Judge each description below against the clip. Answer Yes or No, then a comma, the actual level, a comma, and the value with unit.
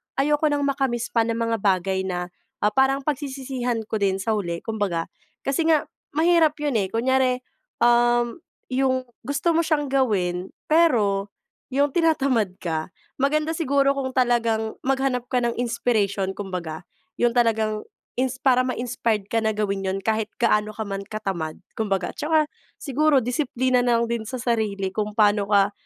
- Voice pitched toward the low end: No, high, 235 Hz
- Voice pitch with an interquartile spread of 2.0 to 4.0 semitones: No, average, 4.5 semitones